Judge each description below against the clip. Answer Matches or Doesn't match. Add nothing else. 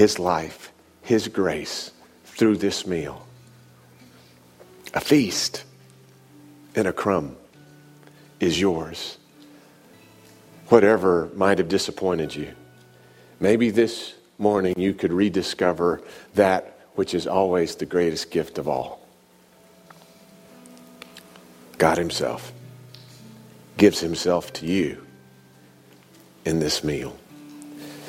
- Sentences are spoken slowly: Matches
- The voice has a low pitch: Matches